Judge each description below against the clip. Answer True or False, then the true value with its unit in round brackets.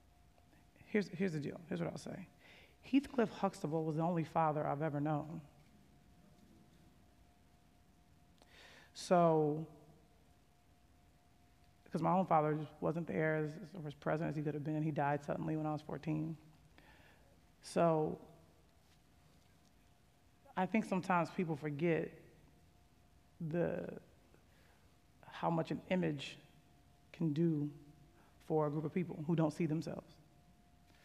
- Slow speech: True (120 wpm)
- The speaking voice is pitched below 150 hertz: False (155 Hz)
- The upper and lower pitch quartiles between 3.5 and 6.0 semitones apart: False (2.5 semitones)